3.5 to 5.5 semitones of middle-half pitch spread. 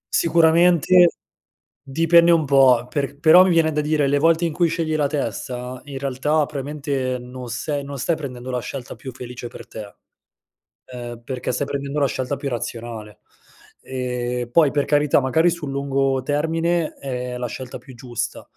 Yes: average, 3.8 semitones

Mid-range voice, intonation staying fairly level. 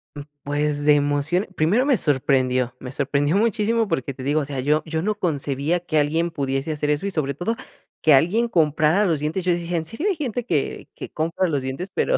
No: medium, 155 Hz; average, 4.2 semitones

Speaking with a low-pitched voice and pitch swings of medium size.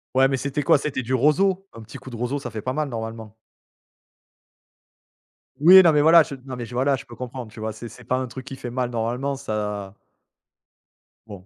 Yes: low, 130 Hz; average, 3.5 semitones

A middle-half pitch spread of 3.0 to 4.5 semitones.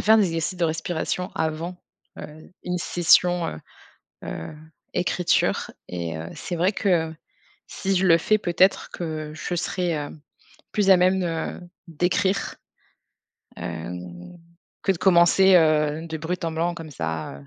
No: narrow, 2.6 semitones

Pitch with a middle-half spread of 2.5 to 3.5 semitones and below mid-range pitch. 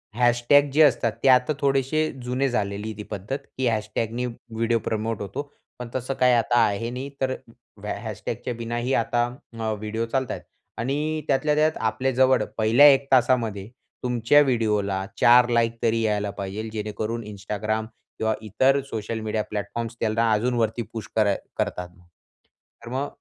Yes: average, 3.1 semitones; low, 115 Hz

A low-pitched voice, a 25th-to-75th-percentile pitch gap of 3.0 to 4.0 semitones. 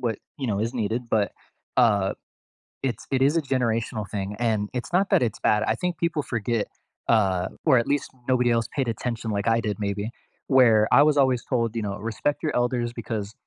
Yes: low, 115 Hz; average, 3.3 semitones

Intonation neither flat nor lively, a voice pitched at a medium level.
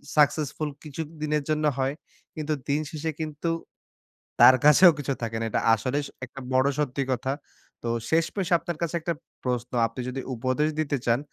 Yes: average, 3.1 semitones; medium, 145 Hz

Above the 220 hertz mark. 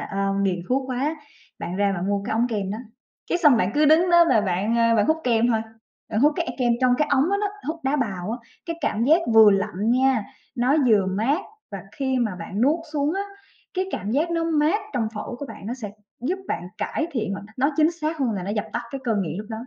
Yes: high, 240 Hz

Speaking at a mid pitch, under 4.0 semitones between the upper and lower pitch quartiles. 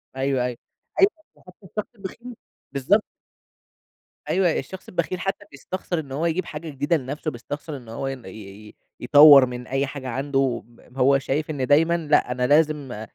No: medium, 145 Hz; average, 4.3 semitones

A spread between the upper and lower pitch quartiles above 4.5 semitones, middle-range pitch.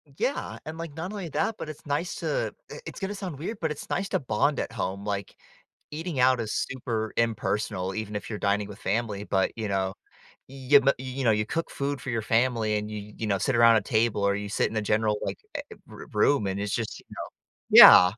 No: wide, 5.4 semitones; low, 115 Hz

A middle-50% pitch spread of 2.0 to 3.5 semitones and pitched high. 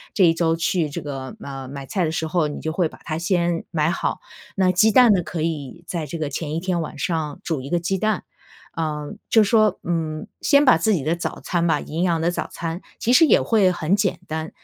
No: average, 2.9 semitones; medium, 165 Hz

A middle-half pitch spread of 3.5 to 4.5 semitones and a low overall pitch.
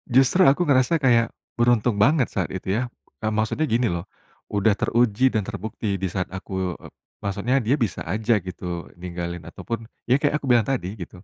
Yes: average, 4.2 semitones; low, 110 Hz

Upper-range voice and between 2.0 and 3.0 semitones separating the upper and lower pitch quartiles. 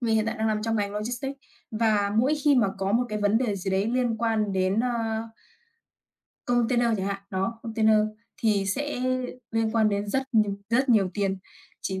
Yes: high, 220 Hz; narrow, 2.6 semitones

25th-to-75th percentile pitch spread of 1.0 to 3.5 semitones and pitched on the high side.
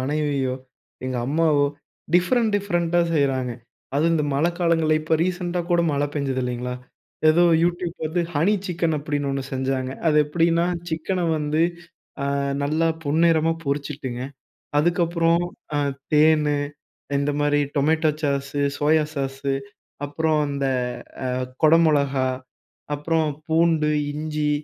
No: average, 2.8 semitones; medium, 150 Hz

